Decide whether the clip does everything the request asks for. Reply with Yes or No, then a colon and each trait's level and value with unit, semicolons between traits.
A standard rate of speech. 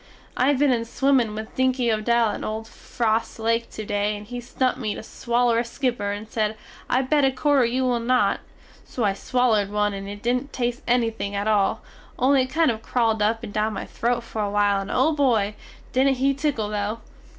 No: fast, 210 wpm